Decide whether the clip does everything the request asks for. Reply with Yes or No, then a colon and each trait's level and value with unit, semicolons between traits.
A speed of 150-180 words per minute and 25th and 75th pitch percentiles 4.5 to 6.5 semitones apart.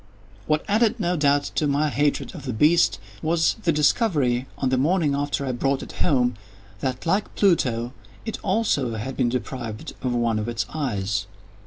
Yes: average, 175 wpm; average, 5.0 semitones